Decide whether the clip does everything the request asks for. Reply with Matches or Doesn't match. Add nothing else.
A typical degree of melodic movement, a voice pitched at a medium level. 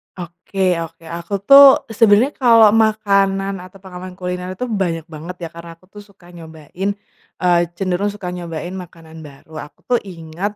Matches